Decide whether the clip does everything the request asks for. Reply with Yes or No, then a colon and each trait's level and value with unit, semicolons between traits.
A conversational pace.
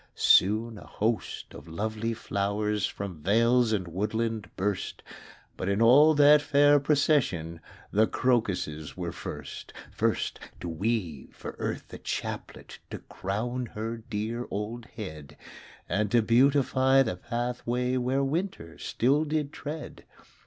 No: slow, 130 wpm